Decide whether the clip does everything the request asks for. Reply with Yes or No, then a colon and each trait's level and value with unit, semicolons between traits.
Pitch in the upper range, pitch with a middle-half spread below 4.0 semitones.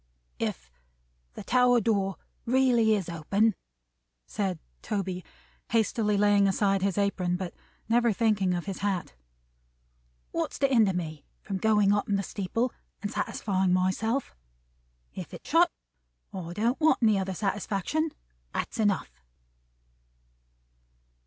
Yes: high, 200 Hz; average, 3.1 semitones